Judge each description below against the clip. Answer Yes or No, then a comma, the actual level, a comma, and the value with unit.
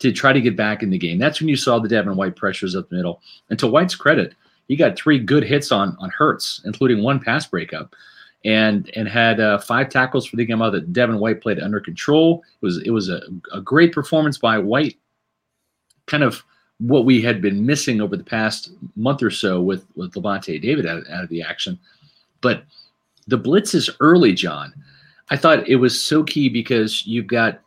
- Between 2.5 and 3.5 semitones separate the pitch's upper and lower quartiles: No, average, 5.0 semitones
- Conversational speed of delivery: No, fast, 210 wpm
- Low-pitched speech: Yes, low, 115 Hz